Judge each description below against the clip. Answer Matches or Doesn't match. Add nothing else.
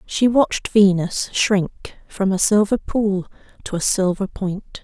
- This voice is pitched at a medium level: Doesn't match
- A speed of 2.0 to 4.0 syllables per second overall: Matches